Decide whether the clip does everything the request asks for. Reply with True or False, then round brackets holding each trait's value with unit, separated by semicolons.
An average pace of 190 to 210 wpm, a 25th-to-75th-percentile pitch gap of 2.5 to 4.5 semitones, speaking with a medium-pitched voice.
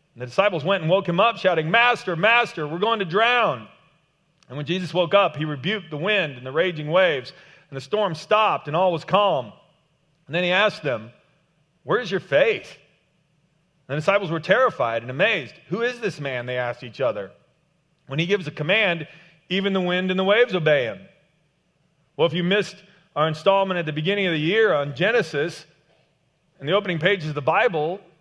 True (200 wpm; 4.1 semitones; 170 Hz)